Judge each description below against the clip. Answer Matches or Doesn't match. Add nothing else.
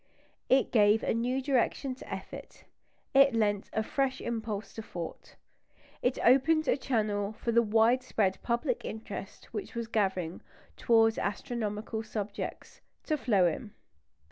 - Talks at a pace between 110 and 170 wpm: Matches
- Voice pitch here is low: Doesn't match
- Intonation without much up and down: Doesn't match